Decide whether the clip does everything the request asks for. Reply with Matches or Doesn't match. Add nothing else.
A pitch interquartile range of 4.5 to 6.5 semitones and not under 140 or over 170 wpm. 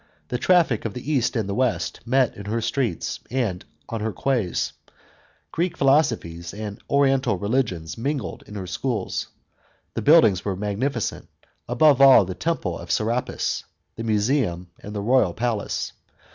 Matches